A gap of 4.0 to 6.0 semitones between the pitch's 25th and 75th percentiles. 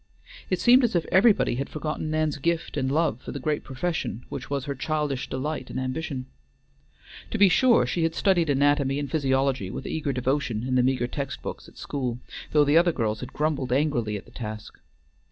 No: average, 3.5 semitones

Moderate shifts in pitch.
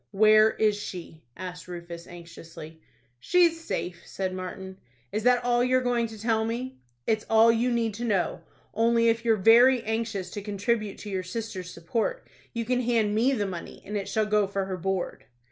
Yes: average, 3.7 semitones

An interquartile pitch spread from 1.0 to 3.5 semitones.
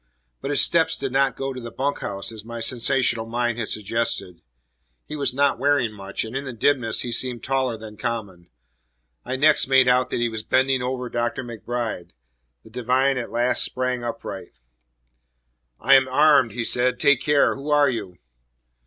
Yes: average, 2.8 semitones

